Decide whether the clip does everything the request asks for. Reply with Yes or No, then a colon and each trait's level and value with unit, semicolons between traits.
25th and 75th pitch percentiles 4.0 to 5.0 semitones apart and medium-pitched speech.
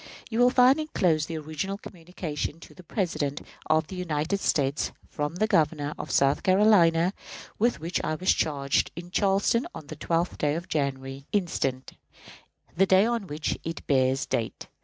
Yes: average, 4.6 semitones; medium, 165 Hz